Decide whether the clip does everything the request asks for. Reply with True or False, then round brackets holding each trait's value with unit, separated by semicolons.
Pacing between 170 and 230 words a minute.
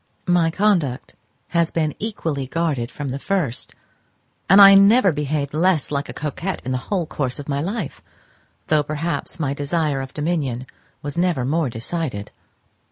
False (160 wpm)